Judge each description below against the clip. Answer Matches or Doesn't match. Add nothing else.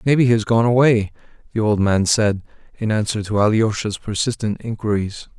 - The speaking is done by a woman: Doesn't match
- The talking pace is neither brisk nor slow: Matches